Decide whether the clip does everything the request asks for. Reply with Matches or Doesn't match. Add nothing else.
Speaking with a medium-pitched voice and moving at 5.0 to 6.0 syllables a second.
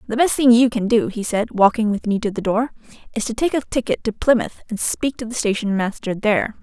Doesn't match